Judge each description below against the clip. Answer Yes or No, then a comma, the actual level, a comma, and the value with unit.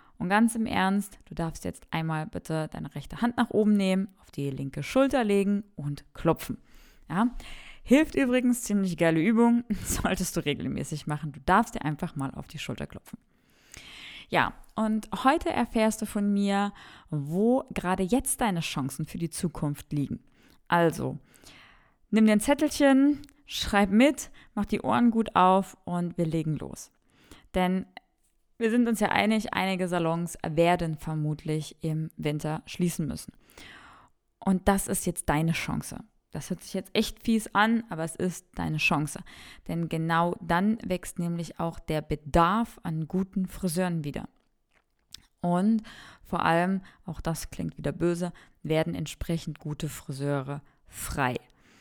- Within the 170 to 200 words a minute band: No, average, 150 wpm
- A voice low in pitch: No, medium, 180 Hz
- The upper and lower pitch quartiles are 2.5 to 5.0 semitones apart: No, wide, 5.4 semitones